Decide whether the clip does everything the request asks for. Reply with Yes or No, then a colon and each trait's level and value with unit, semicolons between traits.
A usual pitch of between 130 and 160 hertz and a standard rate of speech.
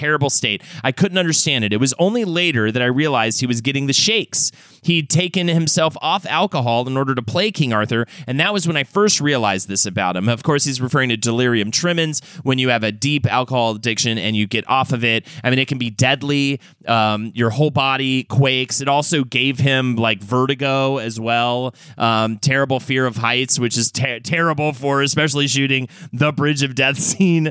No: low, 135 Hz; fast, 210 wpm